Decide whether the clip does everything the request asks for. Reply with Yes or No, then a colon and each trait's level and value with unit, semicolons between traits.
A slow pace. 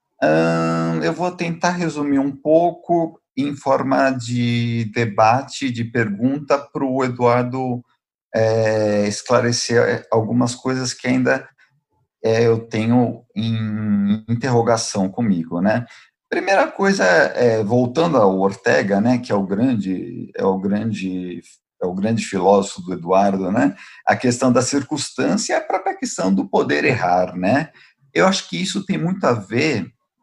No: average, 140 wpm